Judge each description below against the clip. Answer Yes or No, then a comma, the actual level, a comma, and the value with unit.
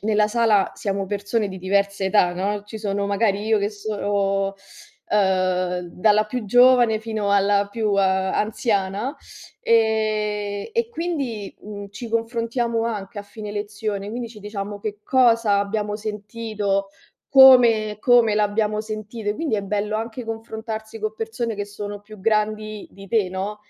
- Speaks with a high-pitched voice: Yes, high, 210 Hz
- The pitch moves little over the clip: Yes, narrow, 1.8 semitones